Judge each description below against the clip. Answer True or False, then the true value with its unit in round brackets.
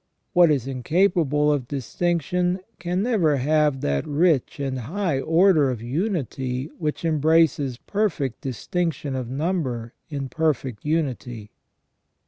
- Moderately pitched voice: True (150 Hz)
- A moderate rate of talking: False (115 wpm)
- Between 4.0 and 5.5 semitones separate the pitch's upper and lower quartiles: True (4.6 semitones)